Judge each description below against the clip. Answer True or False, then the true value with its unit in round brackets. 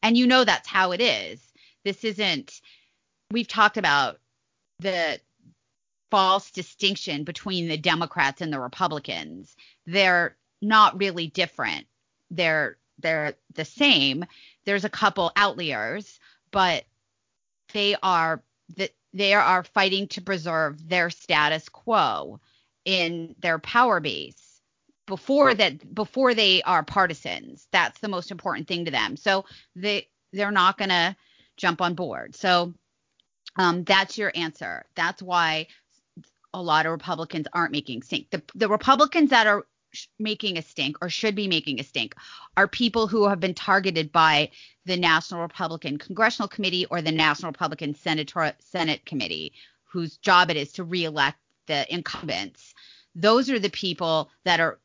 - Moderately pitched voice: True (180 Hz)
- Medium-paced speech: True (145 wpm)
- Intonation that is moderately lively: True (4.1 semitones)